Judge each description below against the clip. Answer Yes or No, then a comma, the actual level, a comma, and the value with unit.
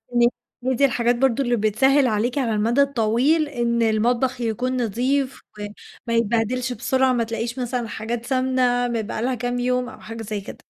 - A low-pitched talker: No, high, 240 Hz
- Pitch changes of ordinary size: No, narrow, 2.1 semitones